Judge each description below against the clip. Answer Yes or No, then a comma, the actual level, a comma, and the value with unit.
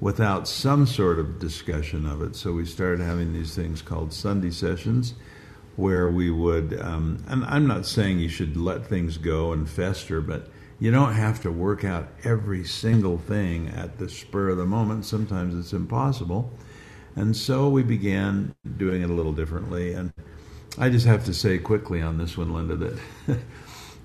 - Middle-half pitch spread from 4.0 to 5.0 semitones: Yes, average, 4.7 semitones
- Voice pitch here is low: Yes, very low, 95 Hz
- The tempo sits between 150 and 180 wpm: Yes, average, 175 wpm